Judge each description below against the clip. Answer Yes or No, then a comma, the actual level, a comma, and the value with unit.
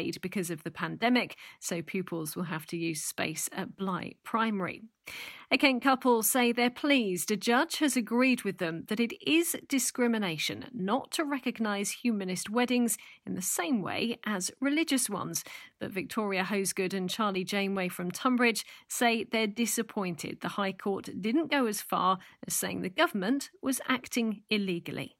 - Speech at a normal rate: Yes, average, 160 wpm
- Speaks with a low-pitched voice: No, high, 220 Hz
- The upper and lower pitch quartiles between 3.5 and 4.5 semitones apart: No, average, 5.0 semitones